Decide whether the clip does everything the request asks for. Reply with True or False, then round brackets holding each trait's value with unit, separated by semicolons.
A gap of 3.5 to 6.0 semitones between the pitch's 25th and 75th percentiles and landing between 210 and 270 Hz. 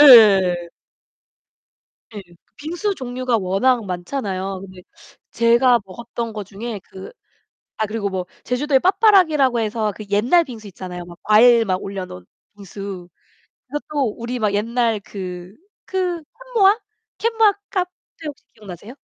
True (5.4 semitones; 225 Hz)